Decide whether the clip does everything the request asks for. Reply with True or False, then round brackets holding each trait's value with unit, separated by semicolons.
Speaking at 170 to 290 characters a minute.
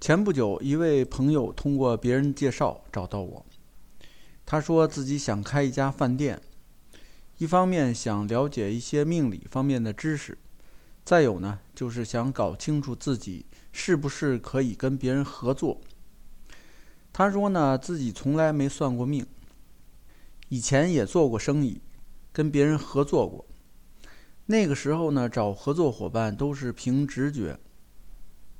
True (210 characters per minute)